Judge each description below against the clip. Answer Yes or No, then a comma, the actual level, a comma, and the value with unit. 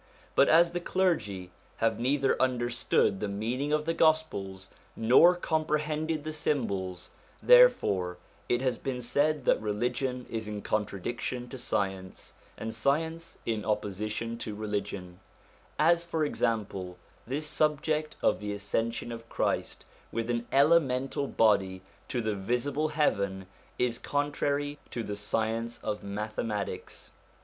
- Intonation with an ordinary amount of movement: No, wide, 6.2 semitones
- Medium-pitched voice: No, low, 120 Hz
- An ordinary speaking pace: No, slow, 130 wpm